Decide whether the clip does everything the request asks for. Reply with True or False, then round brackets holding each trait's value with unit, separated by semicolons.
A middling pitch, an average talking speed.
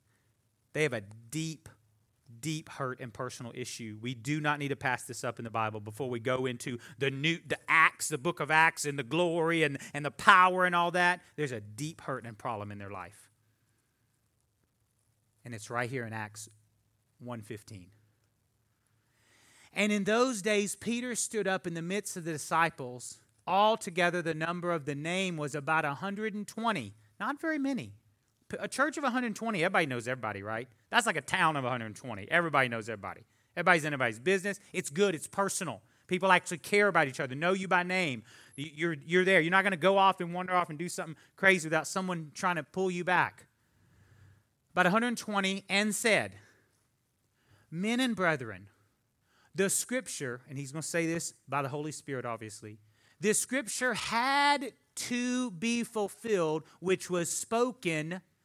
True (155 Hz; 175 wpm)